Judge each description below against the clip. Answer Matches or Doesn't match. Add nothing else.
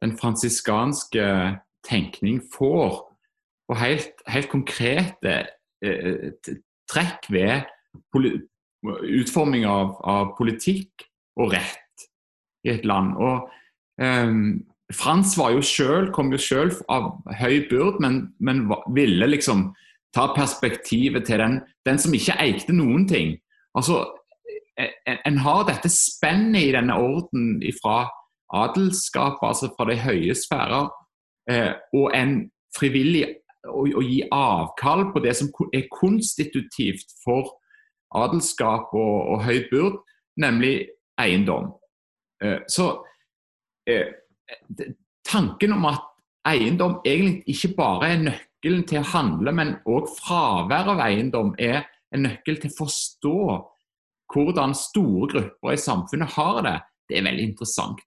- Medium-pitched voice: Matches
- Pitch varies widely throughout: Matches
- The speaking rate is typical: Doesn't match